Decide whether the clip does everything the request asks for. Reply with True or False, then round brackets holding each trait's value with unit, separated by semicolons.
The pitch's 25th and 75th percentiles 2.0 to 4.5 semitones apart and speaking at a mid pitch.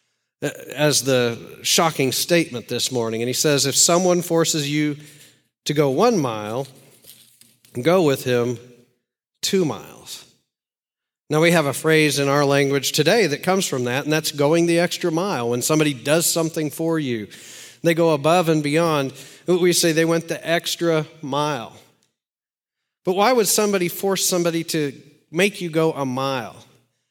True (3.8 semitones; 150 Hz)